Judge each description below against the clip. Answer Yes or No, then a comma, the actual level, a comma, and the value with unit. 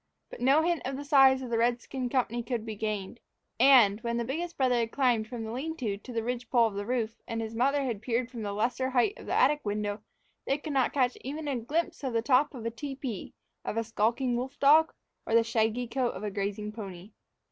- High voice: Yes, high, 240 Hz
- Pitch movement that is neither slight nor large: Yes, average, 3.3 semitones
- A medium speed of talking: No, fast, 245 wpm